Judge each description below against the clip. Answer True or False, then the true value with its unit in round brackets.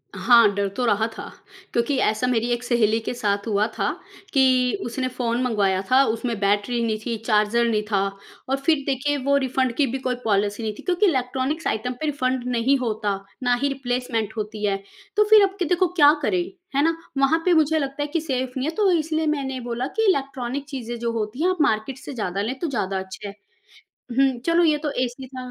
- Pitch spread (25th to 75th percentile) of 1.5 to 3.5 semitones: False (4.0 semitones)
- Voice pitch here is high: True (250 Hz)